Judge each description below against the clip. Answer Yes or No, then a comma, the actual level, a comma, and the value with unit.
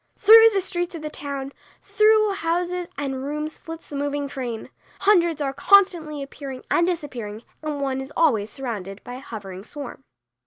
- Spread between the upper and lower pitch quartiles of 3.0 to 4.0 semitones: No, average, 4.5 semitones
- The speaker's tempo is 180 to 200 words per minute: No, average, 165 wpm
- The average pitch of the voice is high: Yes, very high, 290 Hz